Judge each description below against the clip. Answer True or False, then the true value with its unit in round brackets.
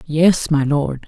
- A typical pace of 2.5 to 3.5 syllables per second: True (3.1 syllables/s)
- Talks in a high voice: False (150 Hz)